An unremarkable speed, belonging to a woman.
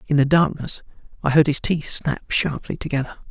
No: average, 180 wpm; male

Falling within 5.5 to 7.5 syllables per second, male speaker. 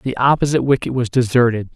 Yes: 6.6 syllables/s; male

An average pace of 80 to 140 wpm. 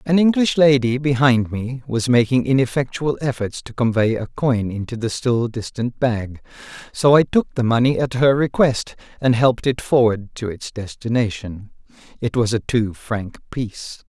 No: average, 165 wpm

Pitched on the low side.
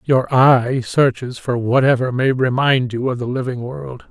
Yes: low, 130 Hz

